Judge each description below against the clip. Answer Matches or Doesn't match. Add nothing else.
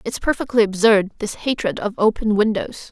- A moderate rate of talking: Matches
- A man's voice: Doesn't match